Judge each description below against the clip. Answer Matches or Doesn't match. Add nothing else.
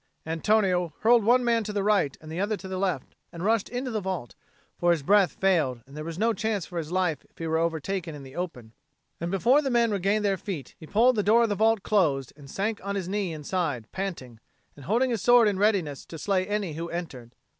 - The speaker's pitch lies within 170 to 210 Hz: Matches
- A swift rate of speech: Matches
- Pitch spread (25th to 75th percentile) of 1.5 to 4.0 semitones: Doesn't match